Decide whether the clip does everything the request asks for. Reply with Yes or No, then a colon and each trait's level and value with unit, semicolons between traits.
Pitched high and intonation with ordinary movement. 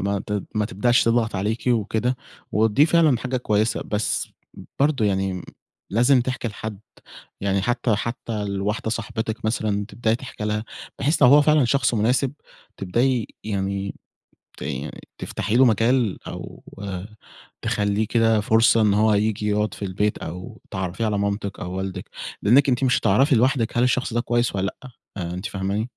No: low, 110 Hz; average, 3.3 semitones